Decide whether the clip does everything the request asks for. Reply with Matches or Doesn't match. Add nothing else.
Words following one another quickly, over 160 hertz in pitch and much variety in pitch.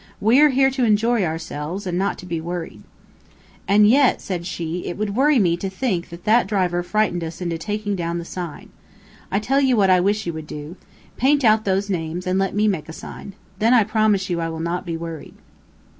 Doesn't match